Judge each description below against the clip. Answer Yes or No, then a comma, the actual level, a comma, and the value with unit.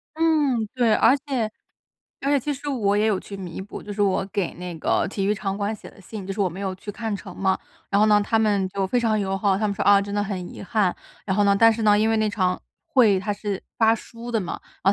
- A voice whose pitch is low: No, high, 205 Hz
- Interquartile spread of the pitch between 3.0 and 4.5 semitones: No, narrow, 2.4 semitones